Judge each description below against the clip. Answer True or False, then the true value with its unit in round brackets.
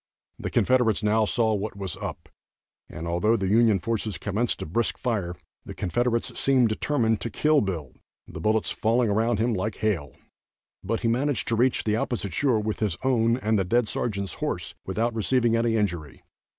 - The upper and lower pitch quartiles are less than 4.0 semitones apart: True (2.9 semitones)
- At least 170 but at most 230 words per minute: True (180 wpm)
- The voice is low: True (110 Hz)